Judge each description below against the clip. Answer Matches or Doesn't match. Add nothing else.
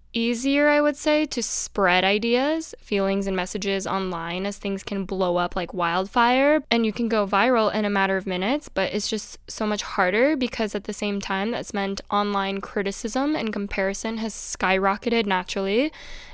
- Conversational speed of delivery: Matches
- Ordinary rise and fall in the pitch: Matches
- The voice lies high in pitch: Matches